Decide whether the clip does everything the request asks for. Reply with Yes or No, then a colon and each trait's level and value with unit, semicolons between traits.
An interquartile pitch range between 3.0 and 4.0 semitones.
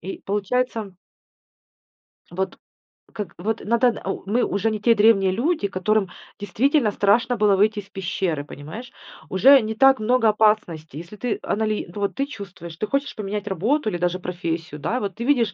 Yes: average, 3.5 semitones